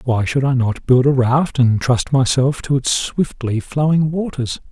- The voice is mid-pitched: No, low, 130 Hz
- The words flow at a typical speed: Yes, average, 190 wpm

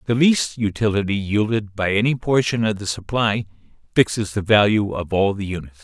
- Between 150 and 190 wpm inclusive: Yes, average, 175 wpm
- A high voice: No, low, 105 Hz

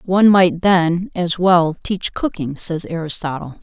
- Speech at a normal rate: Yes, average, 150 wpm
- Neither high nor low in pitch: Yes, medium, 175 Hz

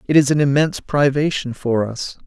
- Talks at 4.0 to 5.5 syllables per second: Yes, 5.4 syllables/s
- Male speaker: Yes, male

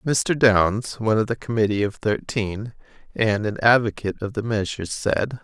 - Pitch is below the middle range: Yes, low, 110 Hz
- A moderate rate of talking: Yes, average, 165 wpm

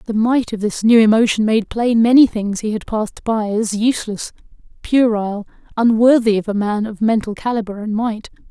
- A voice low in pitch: No, high, 220 Hz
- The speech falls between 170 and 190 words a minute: Yes, average, 185 wpm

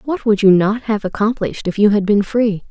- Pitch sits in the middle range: No, high, 210 Hz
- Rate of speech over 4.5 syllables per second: Yes, 5.5 syllables/s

